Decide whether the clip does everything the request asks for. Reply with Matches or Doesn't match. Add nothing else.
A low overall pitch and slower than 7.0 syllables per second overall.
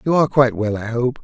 Doesn't match